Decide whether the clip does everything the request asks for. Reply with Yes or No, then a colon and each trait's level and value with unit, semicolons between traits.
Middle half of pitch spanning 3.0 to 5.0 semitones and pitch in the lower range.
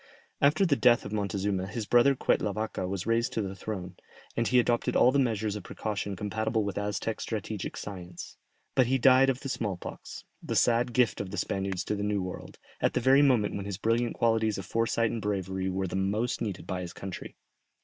Yes: average, 3.3 semitones; low, 105 Hz